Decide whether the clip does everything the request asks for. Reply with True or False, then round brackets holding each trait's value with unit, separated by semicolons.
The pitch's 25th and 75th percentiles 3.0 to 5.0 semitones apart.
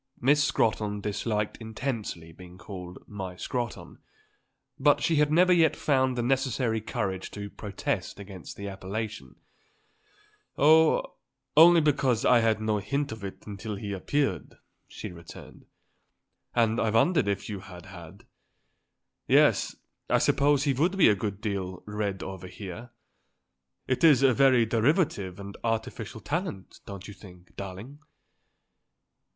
False (5.5 semitones)